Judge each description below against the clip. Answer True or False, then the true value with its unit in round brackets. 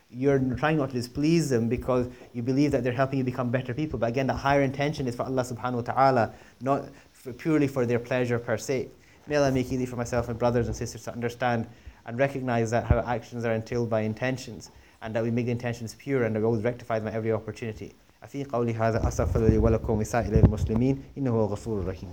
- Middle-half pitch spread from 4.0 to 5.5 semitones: False (2.5 semitones)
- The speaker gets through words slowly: False (195 wpm)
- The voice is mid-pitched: False (120 Hz)